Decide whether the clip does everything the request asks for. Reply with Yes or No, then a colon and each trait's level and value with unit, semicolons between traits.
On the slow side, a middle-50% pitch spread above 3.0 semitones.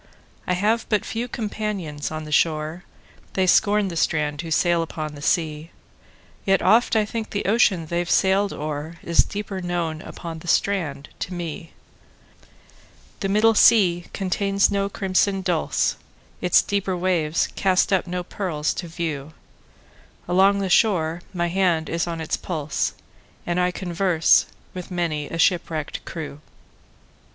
Yes: slow, 130 wpm; average, 3.4 semitones